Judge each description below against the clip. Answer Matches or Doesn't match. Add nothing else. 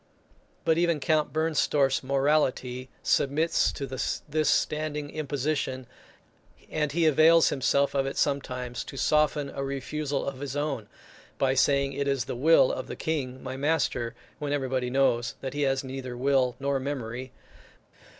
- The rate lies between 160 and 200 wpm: Doesn't match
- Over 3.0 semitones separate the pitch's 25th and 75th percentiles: Doesn't match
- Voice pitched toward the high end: Doesn't match